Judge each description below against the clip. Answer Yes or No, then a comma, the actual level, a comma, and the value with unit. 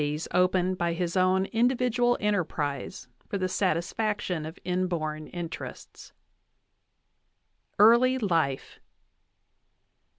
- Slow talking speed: Yes, slow, 90 wpm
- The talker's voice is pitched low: No, medium, 185 Hz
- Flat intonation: No, average, 4.1 semitones